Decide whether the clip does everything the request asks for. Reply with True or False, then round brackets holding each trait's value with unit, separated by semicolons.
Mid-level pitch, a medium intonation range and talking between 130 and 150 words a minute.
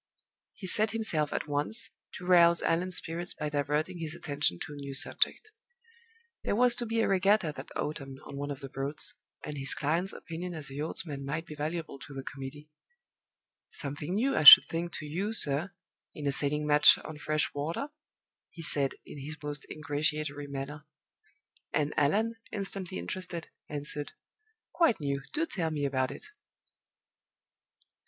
False (150 Hz; 3.5 semitones; 165 wpm)